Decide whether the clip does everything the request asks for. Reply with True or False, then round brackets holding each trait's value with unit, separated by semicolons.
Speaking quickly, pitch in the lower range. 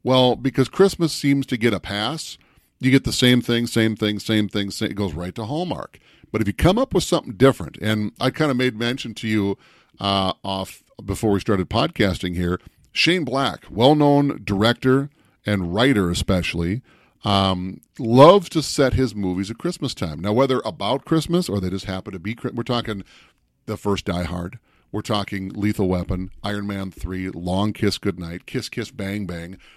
False (185 wpm; 105 Hz)